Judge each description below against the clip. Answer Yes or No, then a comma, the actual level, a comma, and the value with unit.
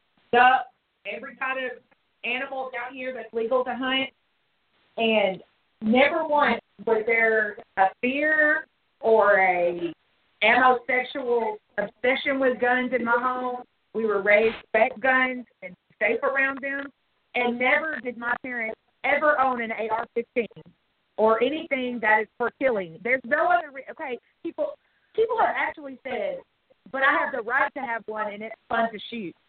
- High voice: Yes, high, 245 Hz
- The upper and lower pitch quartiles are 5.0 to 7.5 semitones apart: No, average, 3.3 semitones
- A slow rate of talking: No, average, 150 wpm